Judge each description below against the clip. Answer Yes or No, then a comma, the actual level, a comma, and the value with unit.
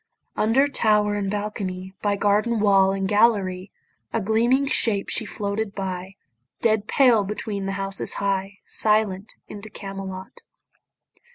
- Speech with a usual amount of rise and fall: No, narrow, 1.9 semitones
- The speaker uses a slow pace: Yes, slow, 125 wpm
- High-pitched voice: Yes, high, 205 Hz